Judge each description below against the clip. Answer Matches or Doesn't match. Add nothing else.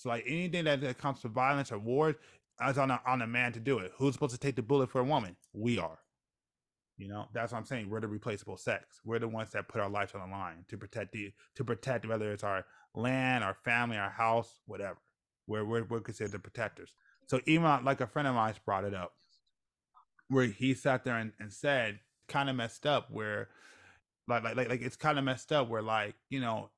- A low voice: Matches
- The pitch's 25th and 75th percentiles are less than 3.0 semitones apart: Doesn't match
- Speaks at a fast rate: Matches